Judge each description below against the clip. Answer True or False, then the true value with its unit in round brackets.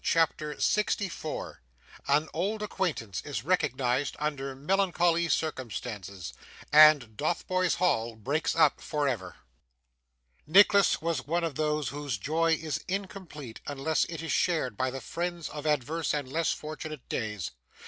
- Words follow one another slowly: True (130 wpm)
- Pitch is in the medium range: True (150 Hz)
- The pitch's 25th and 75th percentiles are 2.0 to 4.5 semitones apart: True (4.2 semitones)